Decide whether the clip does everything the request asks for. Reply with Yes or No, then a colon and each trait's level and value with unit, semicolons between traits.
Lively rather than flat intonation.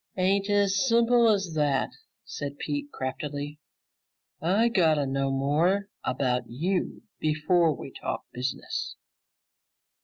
Yes: wide, 6.0 semitones